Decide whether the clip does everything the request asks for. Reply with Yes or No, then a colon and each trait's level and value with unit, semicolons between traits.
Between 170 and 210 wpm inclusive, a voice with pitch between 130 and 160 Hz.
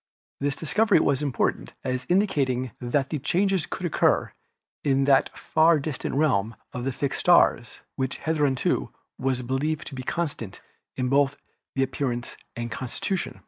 No: average, 145 wpm; low, 135 Hz